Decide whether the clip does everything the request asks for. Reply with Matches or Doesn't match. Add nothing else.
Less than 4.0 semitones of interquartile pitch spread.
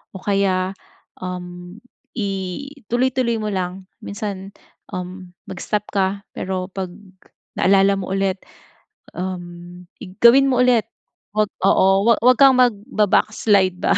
Matches